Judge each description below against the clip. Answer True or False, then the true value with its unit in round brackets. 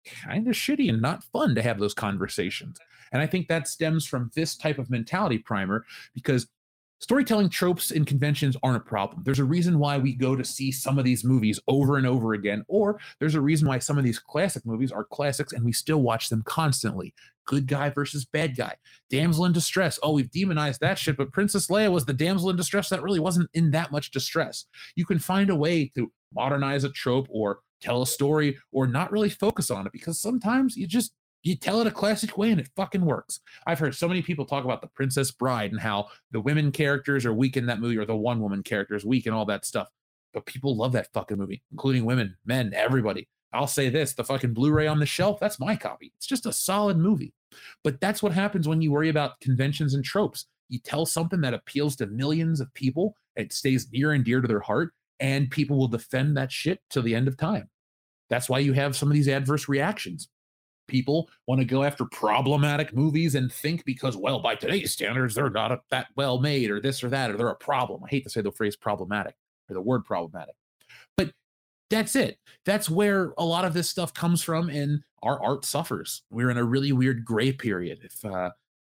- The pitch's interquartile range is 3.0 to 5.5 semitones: True (4.6 semitones)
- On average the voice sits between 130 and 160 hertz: True (140 Hz)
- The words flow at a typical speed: False (220 wpm)